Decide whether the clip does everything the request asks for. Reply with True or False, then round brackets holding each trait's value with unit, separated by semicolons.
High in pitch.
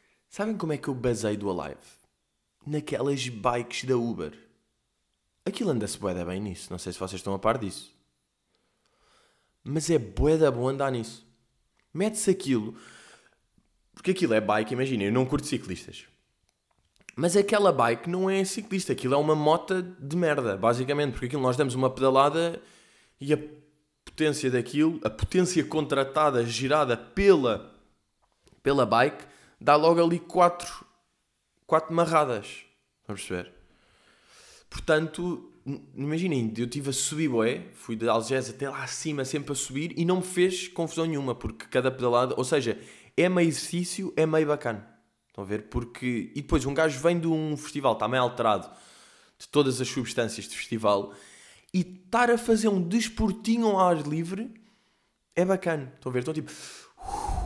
False (145 Hz)